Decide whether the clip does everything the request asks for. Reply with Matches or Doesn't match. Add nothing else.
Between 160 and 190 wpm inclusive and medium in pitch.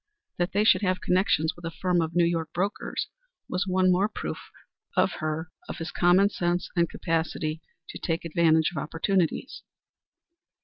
Matches